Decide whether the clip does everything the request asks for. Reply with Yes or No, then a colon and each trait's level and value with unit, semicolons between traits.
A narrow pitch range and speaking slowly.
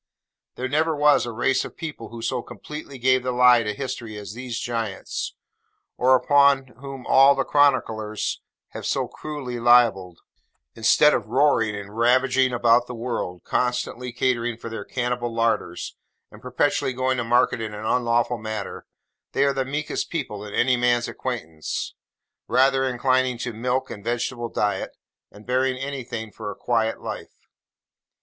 No: narrow, 2.3 semitones; average, 155 wpm